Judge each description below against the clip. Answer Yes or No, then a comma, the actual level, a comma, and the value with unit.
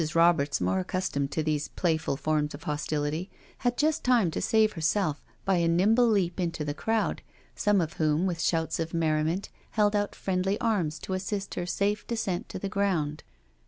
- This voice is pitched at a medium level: Yes, medium, 175 Hz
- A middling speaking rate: Yes, average, 180 wpm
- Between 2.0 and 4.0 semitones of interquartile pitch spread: No, average, 4.7 semitones